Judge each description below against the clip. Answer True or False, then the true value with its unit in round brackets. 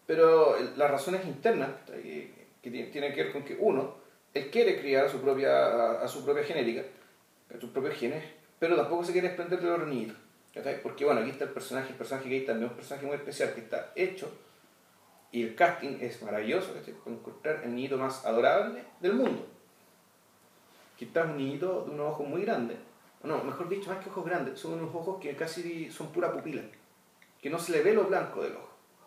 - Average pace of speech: False (200 wpm)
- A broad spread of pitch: True (5.8 semitones)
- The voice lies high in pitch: False (165 Hz)